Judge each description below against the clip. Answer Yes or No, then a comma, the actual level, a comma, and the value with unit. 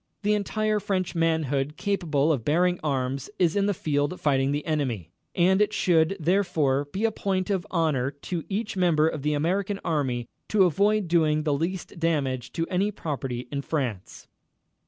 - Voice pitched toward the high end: No, medium, 165 Hz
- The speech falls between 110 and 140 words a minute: No, average, 170 wpm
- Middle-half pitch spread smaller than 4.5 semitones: No, average, 4.9 semitones